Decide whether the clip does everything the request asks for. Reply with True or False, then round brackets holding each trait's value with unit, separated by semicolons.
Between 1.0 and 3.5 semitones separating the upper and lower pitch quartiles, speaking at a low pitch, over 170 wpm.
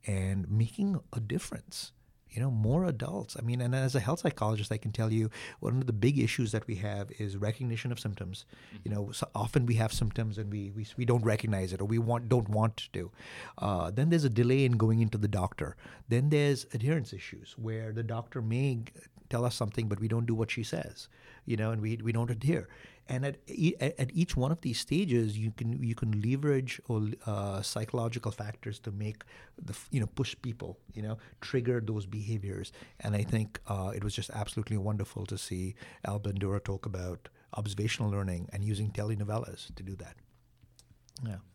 True (2.9 semitones; 115 Hz; 200 wpm)